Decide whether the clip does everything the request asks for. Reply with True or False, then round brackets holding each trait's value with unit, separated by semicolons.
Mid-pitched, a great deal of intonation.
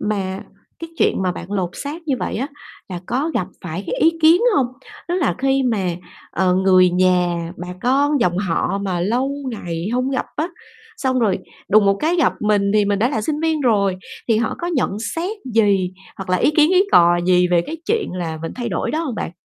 False (210 Hz; 7.2 semitones)